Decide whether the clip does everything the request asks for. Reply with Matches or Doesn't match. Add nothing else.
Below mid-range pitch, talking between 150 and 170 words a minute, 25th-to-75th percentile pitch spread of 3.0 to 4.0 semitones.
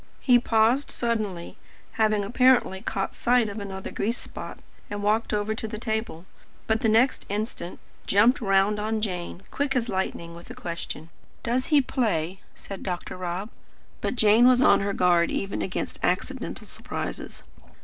Doesn't match